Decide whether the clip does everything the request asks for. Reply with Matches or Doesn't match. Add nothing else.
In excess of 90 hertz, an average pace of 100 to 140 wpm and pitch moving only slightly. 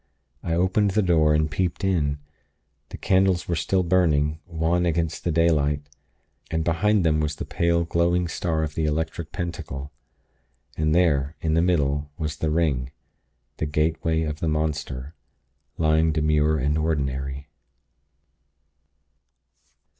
Doesn't match